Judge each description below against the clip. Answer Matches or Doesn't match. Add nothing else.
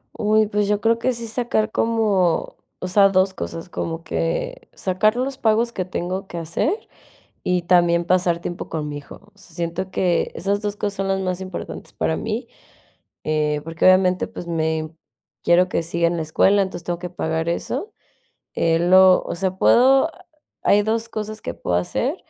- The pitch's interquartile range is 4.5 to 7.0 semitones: Doesn't match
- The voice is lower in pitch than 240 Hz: Matches